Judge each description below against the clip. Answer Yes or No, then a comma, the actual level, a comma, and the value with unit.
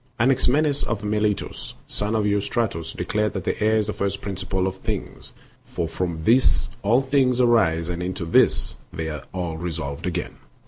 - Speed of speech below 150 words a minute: No, average, 170 wpm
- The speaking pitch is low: Yes, low, 100 Hz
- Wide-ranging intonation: No, average, 4.4 semitones